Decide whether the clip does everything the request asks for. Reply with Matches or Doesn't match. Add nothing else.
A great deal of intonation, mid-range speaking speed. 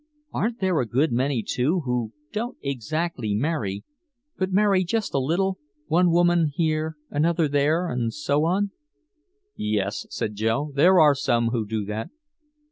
Matches